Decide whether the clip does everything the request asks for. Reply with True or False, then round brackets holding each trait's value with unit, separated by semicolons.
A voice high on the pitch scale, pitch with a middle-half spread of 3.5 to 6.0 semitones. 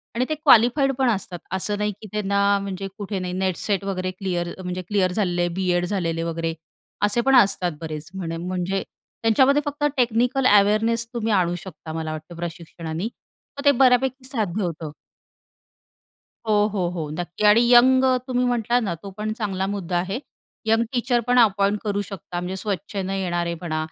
True (200 Hz; 4.7 semitones)